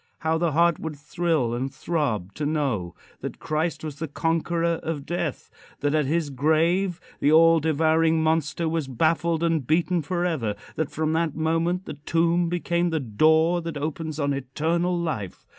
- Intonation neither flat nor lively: No, narrow, 2.3 semitones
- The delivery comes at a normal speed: Yes, average, 165 wpm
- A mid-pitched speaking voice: Yes, medium, 160 Hz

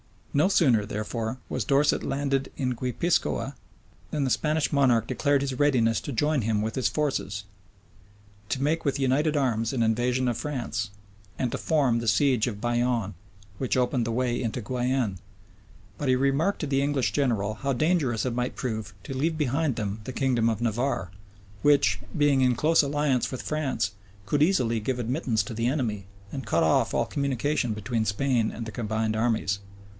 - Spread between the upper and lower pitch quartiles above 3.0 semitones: Yes, average, 3.9 semitones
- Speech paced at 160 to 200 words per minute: Yes, average, 175 wpm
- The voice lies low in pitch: Yes, low, 125 Hz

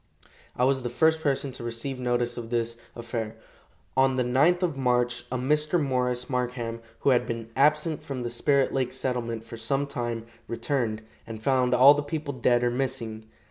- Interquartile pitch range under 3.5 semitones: Yes, narrow, 2.5 semitones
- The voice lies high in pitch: No, low, 125 Hz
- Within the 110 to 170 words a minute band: No, average, 180 wpm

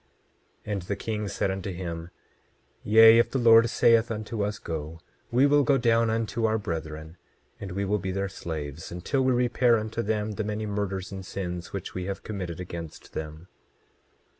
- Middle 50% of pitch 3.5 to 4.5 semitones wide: Yes, average, 4.2 semitones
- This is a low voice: Yes, low, 100 Hz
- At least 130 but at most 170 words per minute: No, average, 185 wpm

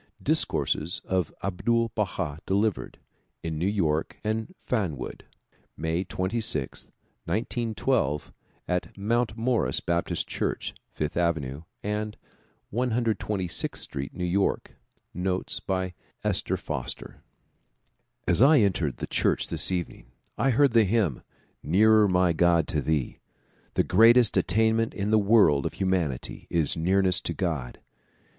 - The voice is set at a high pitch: No, very low, 95 Hz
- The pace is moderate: No, slow, 125 wpm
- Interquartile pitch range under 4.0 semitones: No, average, 5.0 semitones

